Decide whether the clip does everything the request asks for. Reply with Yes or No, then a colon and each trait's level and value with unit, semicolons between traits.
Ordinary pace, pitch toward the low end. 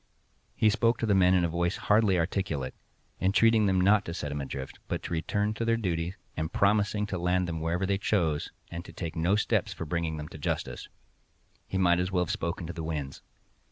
No: fast, 220 wpm; very low, 90 Hz